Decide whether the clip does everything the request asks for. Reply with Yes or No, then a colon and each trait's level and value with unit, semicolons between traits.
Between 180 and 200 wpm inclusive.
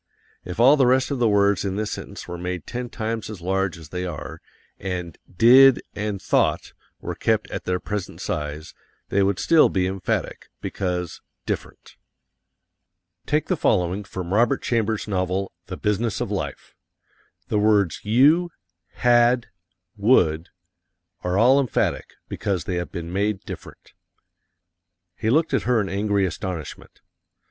No: average, 150 wpm